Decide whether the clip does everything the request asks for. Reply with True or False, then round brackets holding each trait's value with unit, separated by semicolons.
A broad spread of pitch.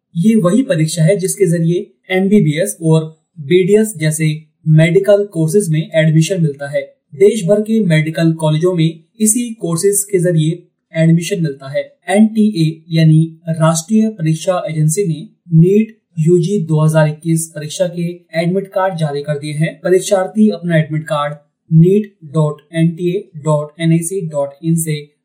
False (3.6 semitones)